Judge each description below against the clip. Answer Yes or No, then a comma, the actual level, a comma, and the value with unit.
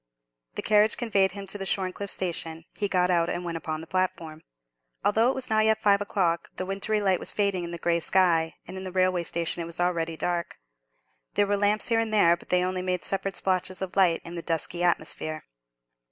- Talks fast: Yes, fast, 220 wpm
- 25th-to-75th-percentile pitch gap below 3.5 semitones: Yes, average, 2.8 semitones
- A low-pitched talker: No, medium, 185 Hz